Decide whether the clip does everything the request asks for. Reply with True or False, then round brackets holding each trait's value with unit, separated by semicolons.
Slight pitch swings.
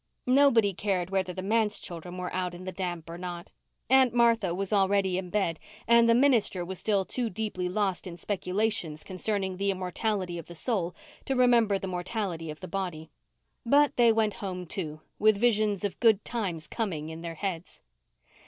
False (3.7 semitones)